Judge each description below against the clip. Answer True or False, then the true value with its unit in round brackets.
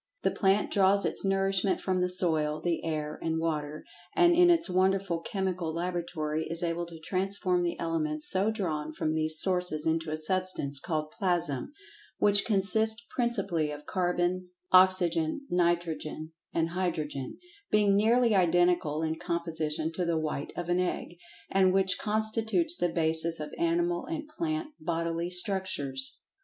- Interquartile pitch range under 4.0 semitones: True (3.3 semitones)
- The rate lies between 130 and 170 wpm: True (150 wpm)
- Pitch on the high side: False (175 Hz)